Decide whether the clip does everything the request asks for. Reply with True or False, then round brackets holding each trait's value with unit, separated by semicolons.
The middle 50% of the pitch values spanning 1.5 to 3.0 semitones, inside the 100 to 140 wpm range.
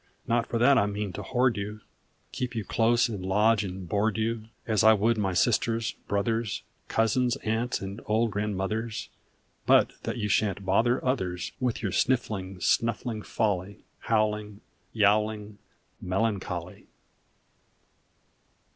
True (2.5 semitones; 135 wpm)